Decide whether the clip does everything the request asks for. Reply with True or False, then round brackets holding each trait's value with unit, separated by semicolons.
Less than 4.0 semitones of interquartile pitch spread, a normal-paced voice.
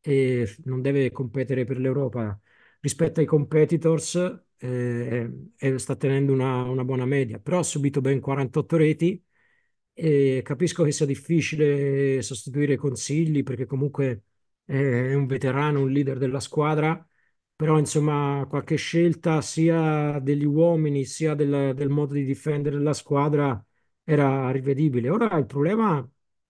True (2.5 semitones; 140 wpm)